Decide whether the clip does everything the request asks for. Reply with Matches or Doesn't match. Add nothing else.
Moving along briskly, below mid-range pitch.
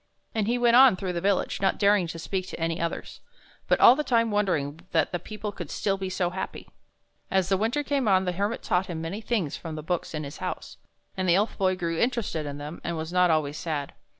Doesn't match